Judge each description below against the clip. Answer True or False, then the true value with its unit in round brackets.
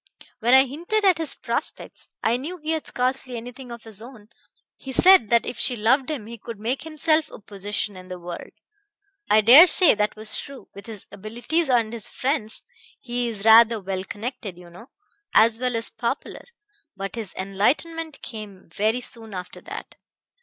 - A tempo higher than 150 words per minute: True (180 wpm)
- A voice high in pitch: True (235 Hz)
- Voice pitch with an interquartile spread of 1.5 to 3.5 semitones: False (4.1 semitones)